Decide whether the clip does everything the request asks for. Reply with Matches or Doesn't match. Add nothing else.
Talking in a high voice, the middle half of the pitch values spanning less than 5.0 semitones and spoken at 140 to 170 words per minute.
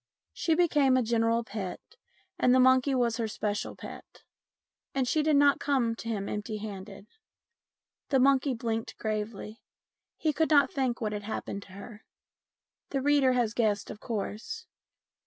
Matches